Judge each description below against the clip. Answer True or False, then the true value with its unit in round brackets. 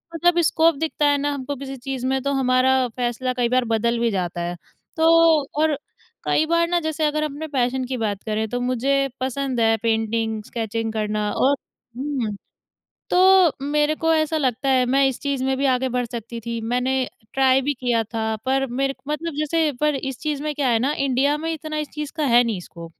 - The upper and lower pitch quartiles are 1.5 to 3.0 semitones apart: False (4.0 semitones)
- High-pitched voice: True (265 Hz)